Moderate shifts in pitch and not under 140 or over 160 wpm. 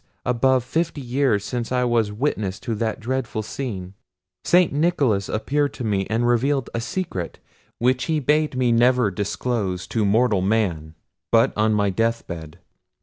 Yes: average, 4.1 semitones; average, 155 wpm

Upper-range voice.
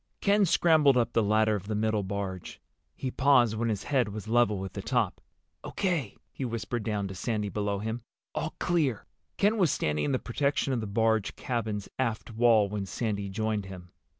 No: low, 110 Hz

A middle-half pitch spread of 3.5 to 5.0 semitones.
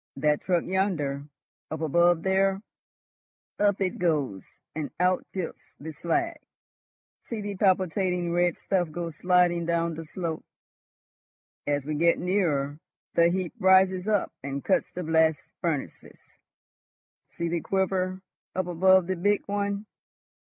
No: average, 2.8 semitones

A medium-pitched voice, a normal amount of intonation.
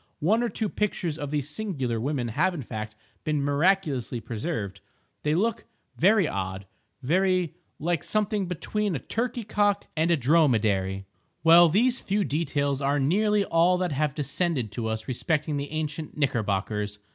No: medium, 150 Hz; wide, 6.6 semitones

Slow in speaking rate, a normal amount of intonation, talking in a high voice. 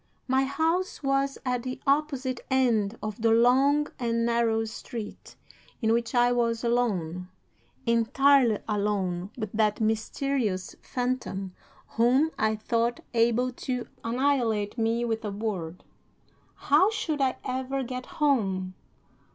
Yes: slow, 125 wpm; average, 3.3 semitones; high, 235 Hz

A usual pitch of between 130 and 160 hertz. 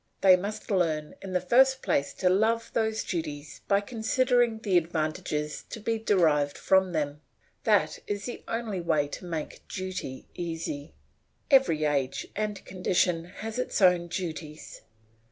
No: medium, 180 Hz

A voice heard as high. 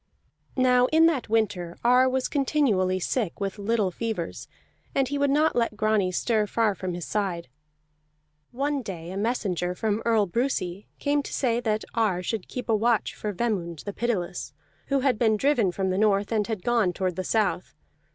Yes: high, 215 Hz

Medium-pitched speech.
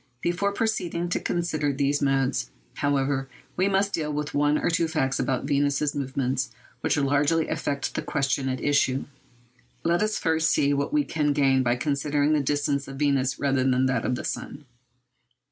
Yes: medium, 145 Hz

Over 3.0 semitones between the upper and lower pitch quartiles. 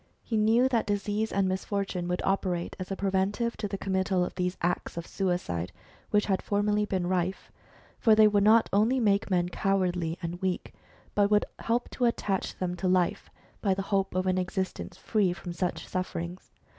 No: narrow, 2.4 semitones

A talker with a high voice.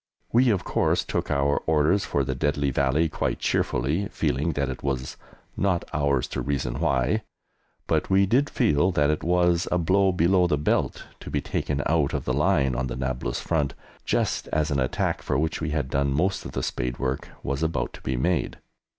No: very low, 75 Hz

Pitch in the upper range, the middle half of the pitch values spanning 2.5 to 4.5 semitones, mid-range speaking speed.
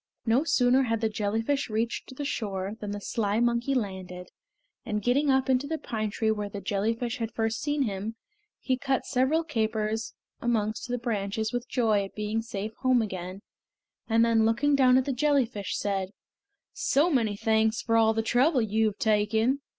Yes: high, 225 Hz; average, 3.2 semitones; average, 180 wpm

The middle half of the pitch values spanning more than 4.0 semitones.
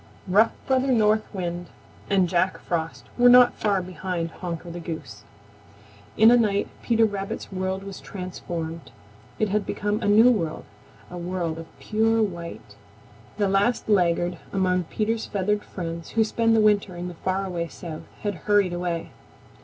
No: average, 3.6 semitones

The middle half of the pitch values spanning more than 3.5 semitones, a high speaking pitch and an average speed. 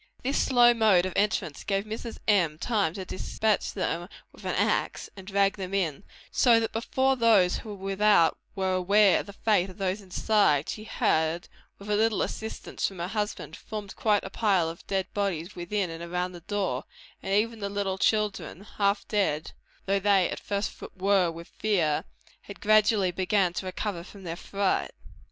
No: average, 2.7 semitones; high, 195 Hz; average, 180 wpm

